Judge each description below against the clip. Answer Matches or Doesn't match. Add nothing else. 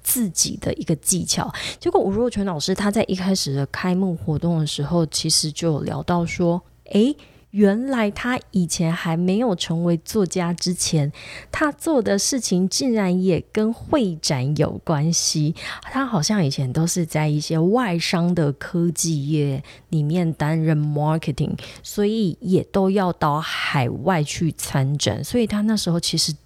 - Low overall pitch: Doesn't match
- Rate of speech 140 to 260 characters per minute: Matches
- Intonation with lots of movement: Doesn't match